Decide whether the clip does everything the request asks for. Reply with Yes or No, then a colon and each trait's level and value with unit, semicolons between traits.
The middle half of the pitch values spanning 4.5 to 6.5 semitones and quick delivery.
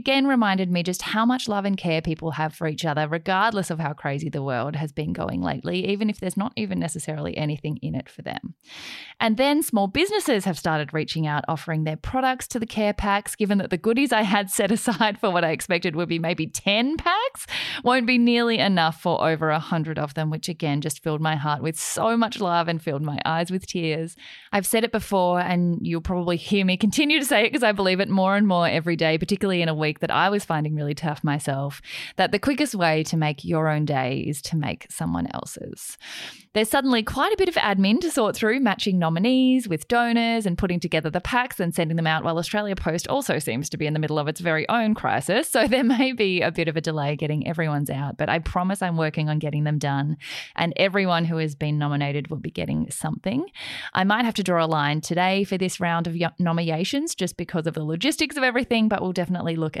Yes: average, 5.2 semitones; fast, 235 wpm